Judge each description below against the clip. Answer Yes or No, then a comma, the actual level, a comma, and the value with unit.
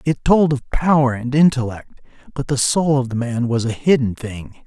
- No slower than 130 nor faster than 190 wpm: No, fast, 205 wpm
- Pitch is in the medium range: No, low, 130 Hz